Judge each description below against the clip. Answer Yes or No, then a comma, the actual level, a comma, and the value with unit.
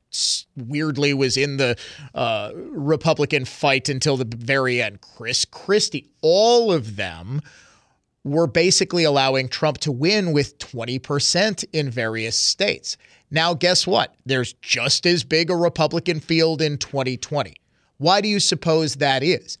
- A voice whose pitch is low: No, medium, 145 Hz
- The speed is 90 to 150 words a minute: Yes, average, 140 wpm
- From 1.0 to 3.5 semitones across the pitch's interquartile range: No, average, 4.1 semitones